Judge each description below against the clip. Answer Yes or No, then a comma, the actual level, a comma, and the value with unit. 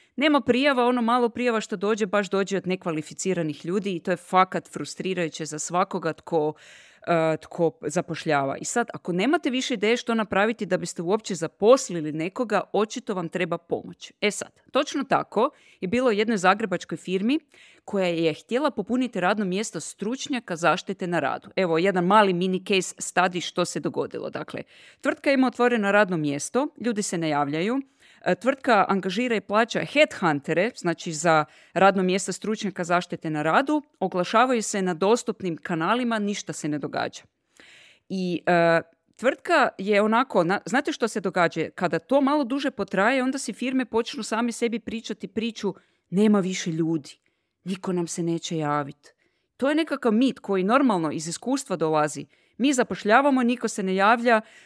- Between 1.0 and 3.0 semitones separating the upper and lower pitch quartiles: No, wide, 5.5 semitones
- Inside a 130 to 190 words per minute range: Yes, fast, 160 wpm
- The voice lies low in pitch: No, high, 195 Hz